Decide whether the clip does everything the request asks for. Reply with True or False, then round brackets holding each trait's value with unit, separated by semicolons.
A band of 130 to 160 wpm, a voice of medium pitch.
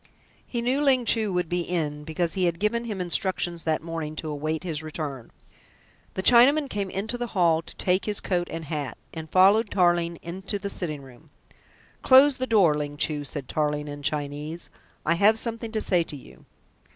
False (190 wpm; 175 Hz)